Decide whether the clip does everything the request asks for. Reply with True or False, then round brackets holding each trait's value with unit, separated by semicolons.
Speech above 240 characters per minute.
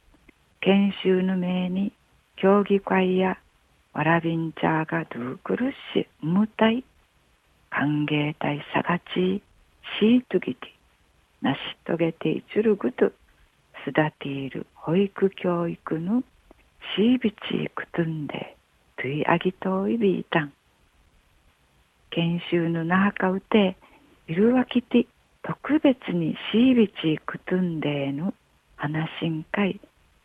False (235 characters per minute)